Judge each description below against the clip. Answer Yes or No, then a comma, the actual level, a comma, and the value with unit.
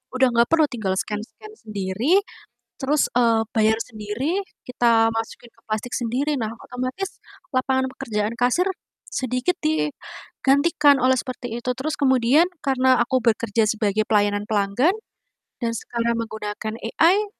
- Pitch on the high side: Yes, high, 235 Hz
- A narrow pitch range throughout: No, average, 3.3 semitones